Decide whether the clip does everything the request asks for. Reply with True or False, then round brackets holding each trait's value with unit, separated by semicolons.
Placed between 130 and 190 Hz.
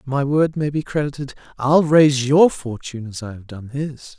True (140 Hz)